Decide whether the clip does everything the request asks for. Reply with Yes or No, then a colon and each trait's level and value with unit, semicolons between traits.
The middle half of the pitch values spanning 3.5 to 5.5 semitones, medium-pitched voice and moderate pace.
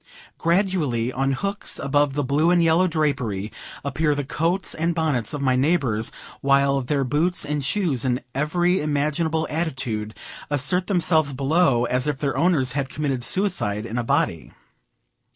Yes: average, 4.1 semitones; medium, 145 Hz; average, 150 wpm